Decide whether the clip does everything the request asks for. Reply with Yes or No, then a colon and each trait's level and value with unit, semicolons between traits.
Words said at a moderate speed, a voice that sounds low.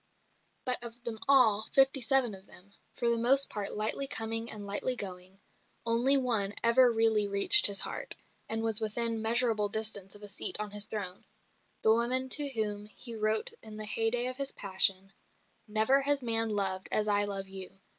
No: average, 185 wpm; high, 220 Hz